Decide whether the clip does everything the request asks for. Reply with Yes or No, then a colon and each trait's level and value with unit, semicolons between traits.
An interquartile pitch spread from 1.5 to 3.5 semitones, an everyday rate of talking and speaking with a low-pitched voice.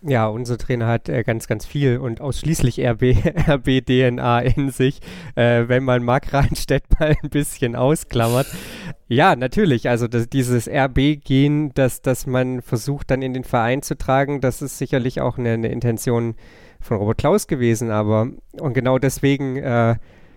Yes: average, 2.8 semitones; average, 160 wpm; low, 130 Hz